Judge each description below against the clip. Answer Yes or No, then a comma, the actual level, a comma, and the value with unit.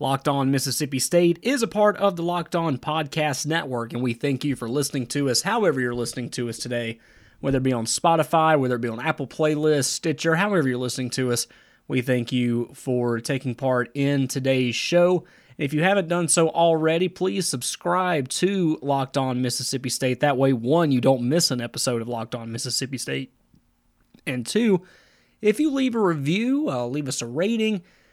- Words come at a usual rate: Yes, average, 195 wpm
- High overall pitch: No, medium, 140 Hz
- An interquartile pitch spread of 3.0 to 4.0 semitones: No, average, 5.1 semitones